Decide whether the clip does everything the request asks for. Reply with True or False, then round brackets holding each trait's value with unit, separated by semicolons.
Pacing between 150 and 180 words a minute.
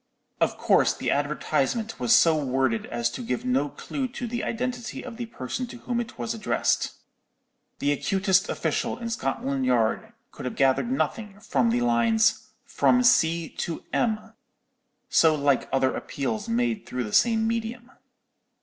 True (160 wpm)